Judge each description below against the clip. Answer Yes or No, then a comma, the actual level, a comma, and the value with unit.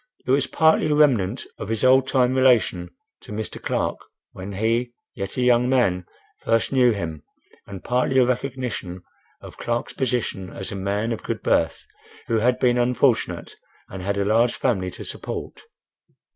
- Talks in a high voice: No, low, 120 Hz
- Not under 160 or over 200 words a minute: Yes, average, 170 wpm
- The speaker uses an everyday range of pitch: Yes, average, 4.3 semitones